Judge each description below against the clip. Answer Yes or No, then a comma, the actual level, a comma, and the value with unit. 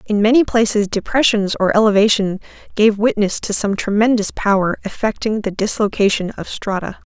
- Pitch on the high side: Yes, high, 210 Hz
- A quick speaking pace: No, average, 145 wpm